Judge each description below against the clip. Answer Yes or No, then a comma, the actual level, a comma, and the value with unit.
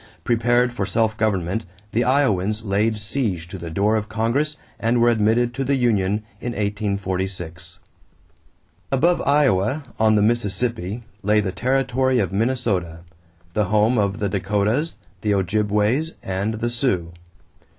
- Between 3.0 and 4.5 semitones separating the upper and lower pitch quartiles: Yes, average, 3.6 semitones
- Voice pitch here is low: Yes, low, 110 Hz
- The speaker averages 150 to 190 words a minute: No, average, 140 wpm